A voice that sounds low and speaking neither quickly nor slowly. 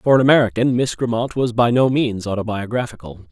Yes: low, 120 Hz; average, 180 wpm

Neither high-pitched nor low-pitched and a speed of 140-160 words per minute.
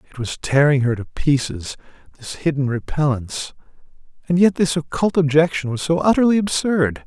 Yes: medium, 150 Hz; average, 155 wpm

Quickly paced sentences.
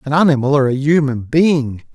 No: average, 185 wpm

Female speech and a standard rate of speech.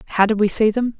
No: female; fast, 300 wpm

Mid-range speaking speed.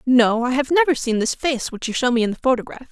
No: fast, 290 wpm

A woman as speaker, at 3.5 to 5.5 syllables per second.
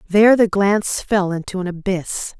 Yes: female; 5.1 syllables/s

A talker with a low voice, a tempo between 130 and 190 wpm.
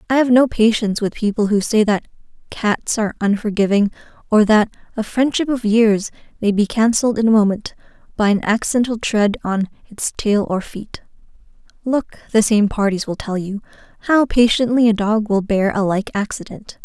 No: high, 215 Hz; average, 175 wpm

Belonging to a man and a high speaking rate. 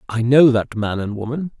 Yes: male; fast, 225 wpm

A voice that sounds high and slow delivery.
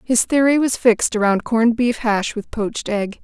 No: high, 230 Hz; fast, 205 wpm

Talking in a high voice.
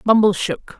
Yes: high, 200 Hz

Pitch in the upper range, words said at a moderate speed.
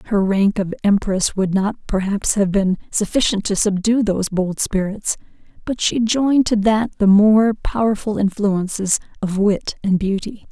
Yes: high, 205 Hz; average, 160 wpm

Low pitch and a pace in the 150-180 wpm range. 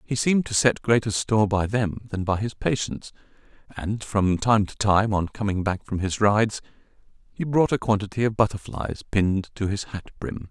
No: low, 105 Hz; average, 195 wpm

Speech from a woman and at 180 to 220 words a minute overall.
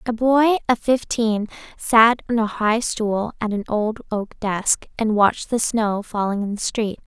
Yes: female; average, 185 wpm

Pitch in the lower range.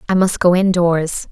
No: medium, 180 Hz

